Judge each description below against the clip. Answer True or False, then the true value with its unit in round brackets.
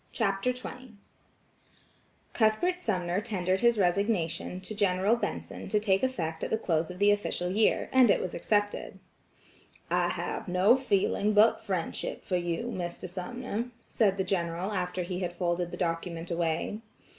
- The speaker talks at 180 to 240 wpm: False (155 wpm)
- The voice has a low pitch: False (190 Hz)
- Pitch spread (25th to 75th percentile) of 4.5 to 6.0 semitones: False (3.5 semitones)